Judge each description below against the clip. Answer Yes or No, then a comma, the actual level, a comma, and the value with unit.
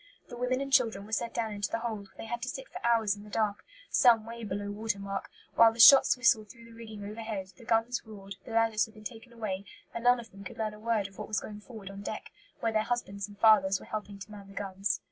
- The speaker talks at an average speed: No, fast, 265 wpm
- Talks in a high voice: Yes, high, 220 Hz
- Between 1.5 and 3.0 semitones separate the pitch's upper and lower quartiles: Yes, narrow, 2.4 semitones